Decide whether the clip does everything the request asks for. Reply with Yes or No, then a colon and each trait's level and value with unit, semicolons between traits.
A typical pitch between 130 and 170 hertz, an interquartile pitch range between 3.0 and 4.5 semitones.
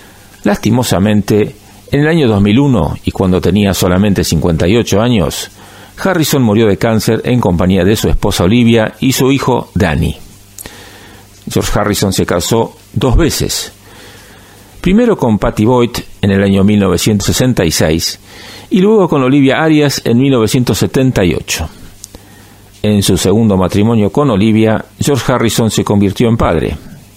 No: low, 105 Hz; average, 3.4 semitones